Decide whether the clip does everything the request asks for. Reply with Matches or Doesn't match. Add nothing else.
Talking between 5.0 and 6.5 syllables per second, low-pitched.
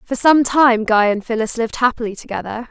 Doesn't match